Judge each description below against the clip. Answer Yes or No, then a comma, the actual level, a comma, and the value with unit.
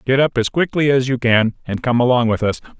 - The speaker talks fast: Yes, fast, 260 wpm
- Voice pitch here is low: Yes, low, 125 Hz